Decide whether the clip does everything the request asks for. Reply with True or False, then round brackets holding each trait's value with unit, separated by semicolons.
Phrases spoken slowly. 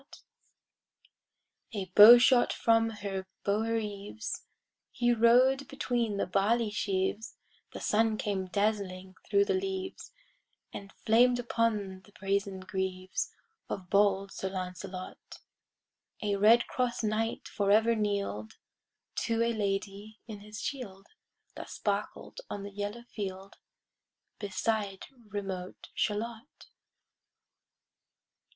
True (115 wpm)